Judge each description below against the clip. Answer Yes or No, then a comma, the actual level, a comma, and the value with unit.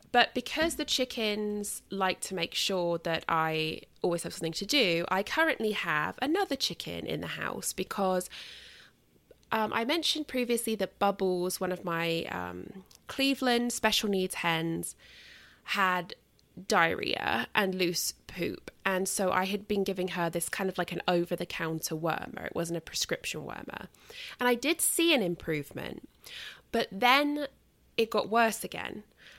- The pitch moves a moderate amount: No, wide, 6.0 semitones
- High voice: Yes, high, 195 Hz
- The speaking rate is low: No, average, 155 wpm